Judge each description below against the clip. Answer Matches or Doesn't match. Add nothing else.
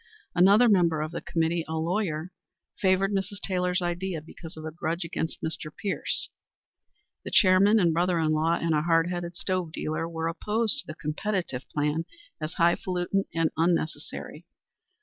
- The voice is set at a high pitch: Doesn't match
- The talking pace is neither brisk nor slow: Matches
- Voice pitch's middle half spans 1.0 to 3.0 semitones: Matches